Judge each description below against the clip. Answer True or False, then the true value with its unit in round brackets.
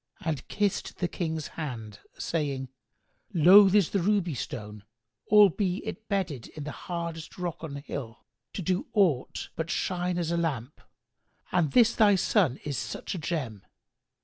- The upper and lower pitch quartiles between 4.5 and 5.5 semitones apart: True (4.9 semitones)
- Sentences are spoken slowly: False (155 wpm)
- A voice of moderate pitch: True (165 Hz)